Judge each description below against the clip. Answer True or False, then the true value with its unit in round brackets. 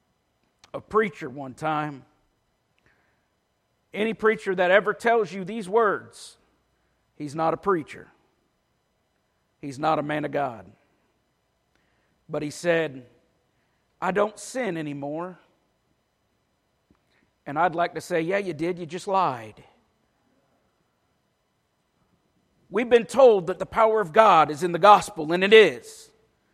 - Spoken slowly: True (125 wpm)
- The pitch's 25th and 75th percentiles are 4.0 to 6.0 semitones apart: True (5.1 semitones)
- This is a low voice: False (180 Hz)